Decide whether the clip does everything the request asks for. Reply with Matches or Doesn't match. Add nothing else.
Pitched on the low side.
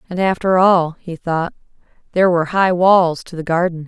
Doesn't match